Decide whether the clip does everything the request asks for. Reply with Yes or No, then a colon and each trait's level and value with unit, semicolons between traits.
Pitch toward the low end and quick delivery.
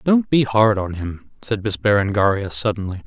No: low, 105 Hz; average, 175 wpm